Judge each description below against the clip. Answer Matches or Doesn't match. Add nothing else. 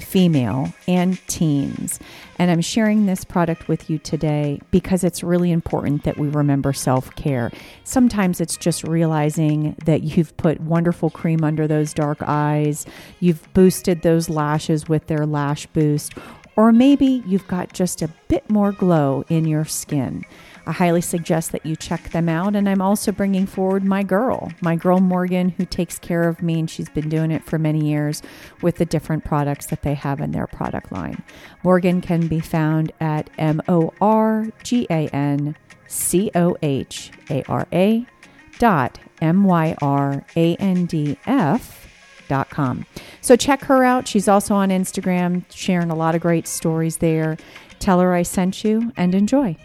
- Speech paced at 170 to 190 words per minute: Doesn't match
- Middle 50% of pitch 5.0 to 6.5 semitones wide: Doesn't match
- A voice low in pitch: Doesn't match